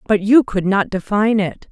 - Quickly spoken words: Yes, fast, 210 wpm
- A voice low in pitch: No, high, 200 Hz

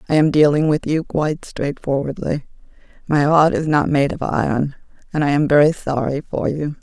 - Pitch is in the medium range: Yes, medium, 145 Hz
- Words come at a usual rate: Yes, average, 185 wpm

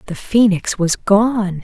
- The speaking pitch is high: Yes, high, 195 Hz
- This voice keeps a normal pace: Yes, average, 145 wpm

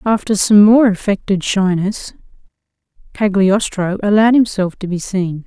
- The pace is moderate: No, slow, 120 wpm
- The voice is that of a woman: Yes, female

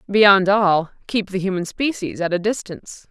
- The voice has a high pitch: Yes, high, 195 Hz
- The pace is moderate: Yes, average, 175 wpm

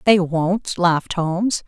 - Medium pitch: Yes, medium, 180 Hz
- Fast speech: No, average, 145 wpm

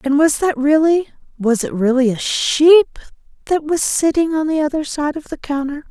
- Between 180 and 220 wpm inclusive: Yes, average, 185 wpm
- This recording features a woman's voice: Yes, female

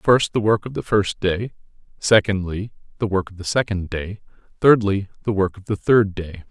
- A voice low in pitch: Yes, low, 100 Hz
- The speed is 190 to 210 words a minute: Yes, average, 195 wpm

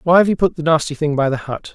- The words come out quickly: Yes, fast, 345 wpm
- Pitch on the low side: No, medium, 155 Hz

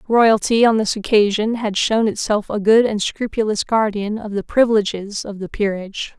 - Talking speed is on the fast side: No, average, 175 wpm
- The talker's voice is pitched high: Yes, high, 215 Hz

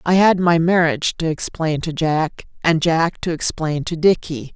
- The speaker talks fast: No, average, 185 wpm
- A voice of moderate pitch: Yes, medium, 165 Hz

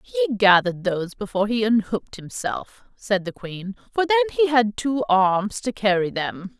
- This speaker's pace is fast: No, average, 175 wpm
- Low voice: No, high, 215 Hz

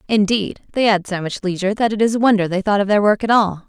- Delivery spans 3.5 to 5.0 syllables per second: No, 6.6 syllables/s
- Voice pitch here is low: No, high, 205 Hz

